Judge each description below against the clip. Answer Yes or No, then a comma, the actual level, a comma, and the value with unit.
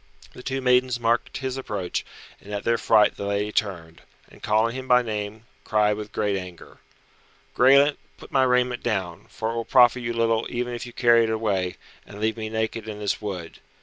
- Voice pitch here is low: Yes, low, 110 Hz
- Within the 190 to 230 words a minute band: Yes, average, 200 wpm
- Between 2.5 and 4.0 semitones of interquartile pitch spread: Yes, average, 2.9 semitones